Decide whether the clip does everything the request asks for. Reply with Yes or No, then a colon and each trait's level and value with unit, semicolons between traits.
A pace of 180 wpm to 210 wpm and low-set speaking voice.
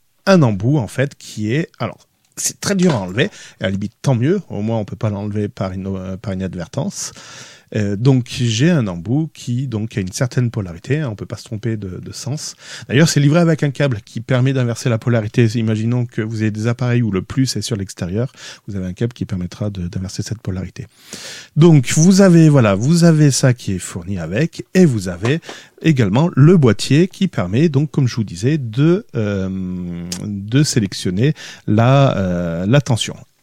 Yes: average, 200 wpm; low, 120 Hz